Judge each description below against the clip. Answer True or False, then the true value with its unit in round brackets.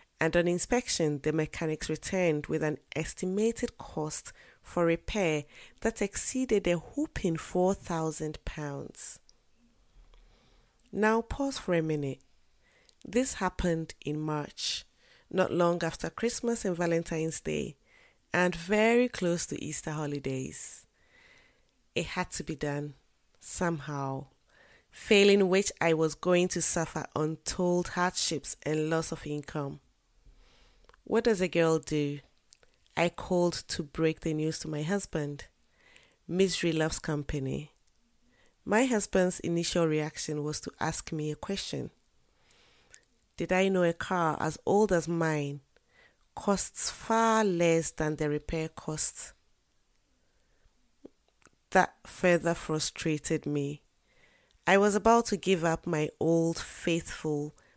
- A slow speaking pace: True (120 wpm)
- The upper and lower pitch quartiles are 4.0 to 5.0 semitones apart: False (3.3 semitones)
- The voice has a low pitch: False (165 Hz)